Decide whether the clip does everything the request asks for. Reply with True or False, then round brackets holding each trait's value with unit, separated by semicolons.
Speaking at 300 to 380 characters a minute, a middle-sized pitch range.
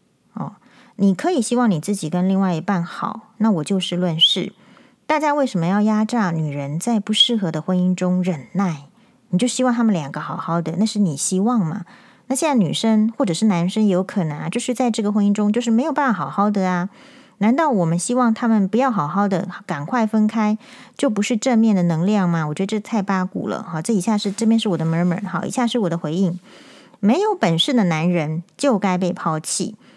True (320 characters per minute; 4.6 semitones)